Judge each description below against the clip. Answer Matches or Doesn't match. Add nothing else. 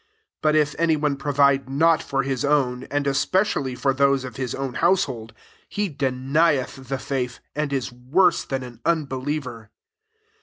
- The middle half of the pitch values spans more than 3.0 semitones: Doesn't match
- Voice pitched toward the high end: Doesn't match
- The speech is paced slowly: Doesn't match